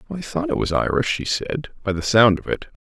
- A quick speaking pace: Yes, fast, 255 wpm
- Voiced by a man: Yes, male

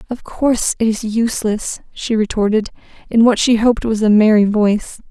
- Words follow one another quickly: No, average, 175 wpm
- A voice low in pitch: No, high, 220 Hz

